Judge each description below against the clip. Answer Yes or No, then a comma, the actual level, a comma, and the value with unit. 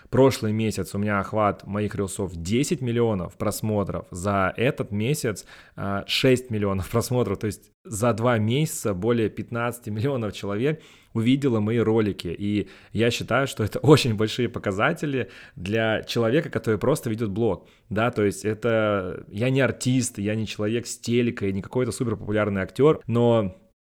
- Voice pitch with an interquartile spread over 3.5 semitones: No, average, 3.0 semitones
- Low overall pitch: Yes, low, 110 Hz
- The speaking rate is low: No, average, 150 wpm